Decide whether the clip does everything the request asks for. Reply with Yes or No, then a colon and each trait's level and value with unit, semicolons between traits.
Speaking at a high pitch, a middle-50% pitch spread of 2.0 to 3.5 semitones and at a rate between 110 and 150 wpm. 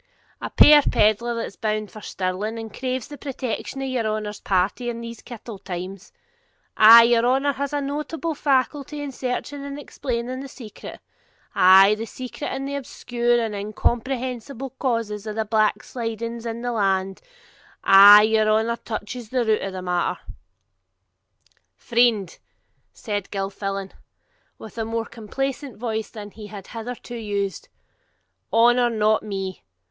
Yes: high, 230 Hz; average, 3.2 semitones; average, 140 wpm